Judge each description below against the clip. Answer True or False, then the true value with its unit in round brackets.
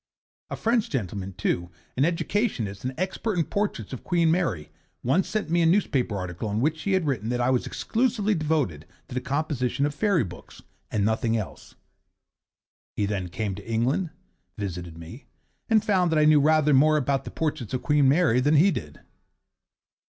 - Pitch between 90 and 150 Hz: True (140 Hz)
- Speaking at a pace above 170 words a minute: True (180 wpm)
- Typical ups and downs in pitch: False (7.8 semitones)